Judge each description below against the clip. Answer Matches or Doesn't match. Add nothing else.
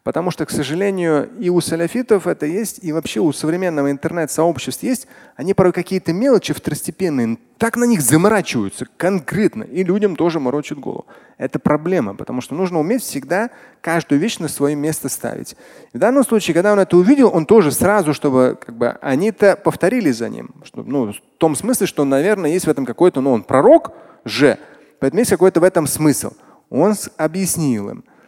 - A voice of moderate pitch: Matches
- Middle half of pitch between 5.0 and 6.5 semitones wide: Matches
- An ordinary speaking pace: Doesn't match